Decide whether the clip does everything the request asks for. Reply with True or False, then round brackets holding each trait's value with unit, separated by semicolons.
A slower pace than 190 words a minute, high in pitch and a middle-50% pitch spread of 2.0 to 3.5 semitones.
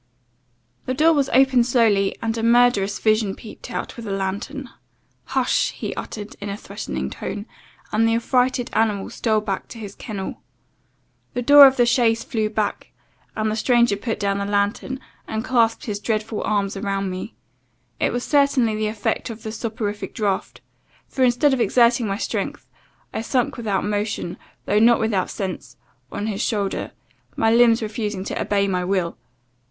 True (170 wpm; 220 Hz; 3.0 semitones)